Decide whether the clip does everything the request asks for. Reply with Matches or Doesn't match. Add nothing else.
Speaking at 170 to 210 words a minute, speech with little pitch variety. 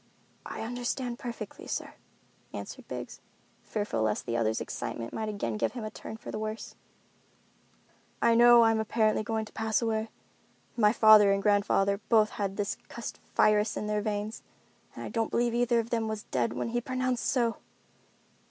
Matches